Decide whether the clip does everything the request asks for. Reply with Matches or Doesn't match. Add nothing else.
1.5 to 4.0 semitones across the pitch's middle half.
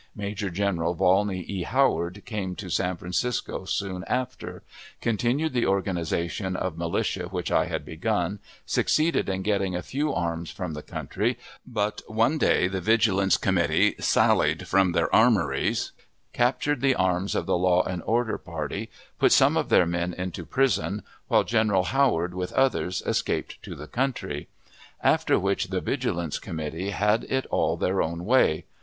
Doesn't match